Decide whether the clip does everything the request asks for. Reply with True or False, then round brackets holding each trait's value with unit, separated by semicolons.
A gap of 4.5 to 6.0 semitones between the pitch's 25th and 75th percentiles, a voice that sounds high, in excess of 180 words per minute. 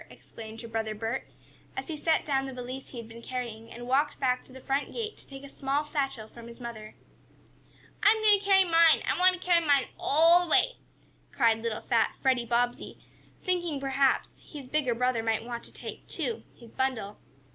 True (4.8 semitones; 265 Hz; 200 wpm)